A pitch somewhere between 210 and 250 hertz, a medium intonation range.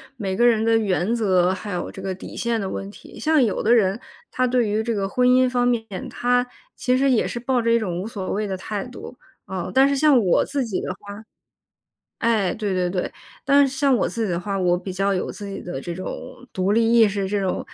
Yes: high, 215 Hz; average, 4.3 semitones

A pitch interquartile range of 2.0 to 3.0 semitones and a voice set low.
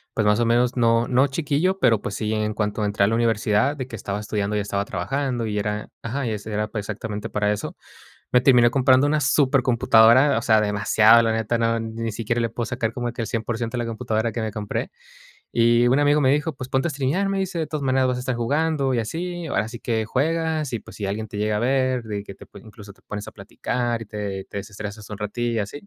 No: average, 3.6 semitones; low, 115 Hz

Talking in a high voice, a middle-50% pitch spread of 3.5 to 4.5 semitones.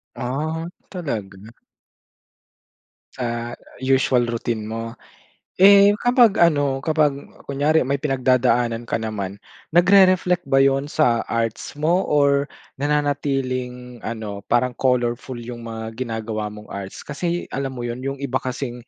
No: low, 130 Hz; average, 4.0 semitones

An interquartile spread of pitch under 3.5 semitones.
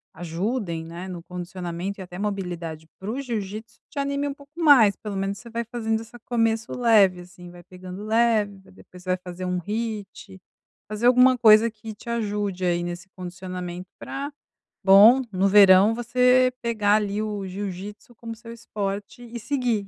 No: average, 4.1 semitones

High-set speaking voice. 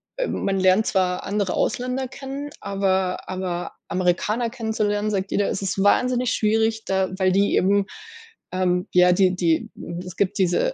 Yes: high, 195 Hz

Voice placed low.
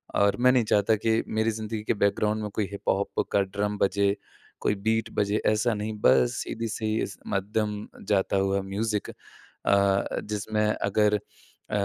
Yes: low, 105 Hz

